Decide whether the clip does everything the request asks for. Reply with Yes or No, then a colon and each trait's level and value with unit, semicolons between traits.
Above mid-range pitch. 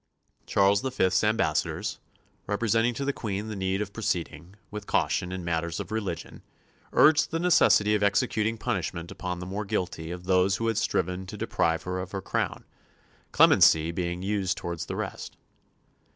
No: very low, 95 Hz